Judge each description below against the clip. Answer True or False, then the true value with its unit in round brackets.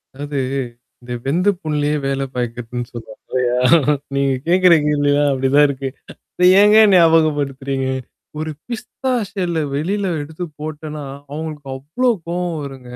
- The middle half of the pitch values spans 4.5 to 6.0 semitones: False (3.7 semitones)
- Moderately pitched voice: True (145 Hz)